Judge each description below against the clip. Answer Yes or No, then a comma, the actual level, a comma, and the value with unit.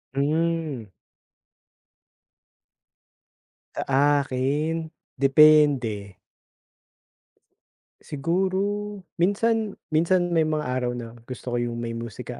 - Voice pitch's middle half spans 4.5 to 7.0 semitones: Yes, average, 4.9 semitones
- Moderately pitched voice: Yes, medium, 150 Hz